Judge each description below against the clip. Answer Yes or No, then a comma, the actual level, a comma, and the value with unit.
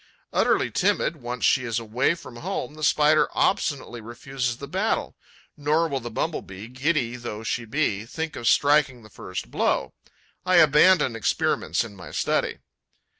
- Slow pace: No, average, 160 wpm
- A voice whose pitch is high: No, low, 130 Hz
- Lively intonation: No, average, 4.8 semitones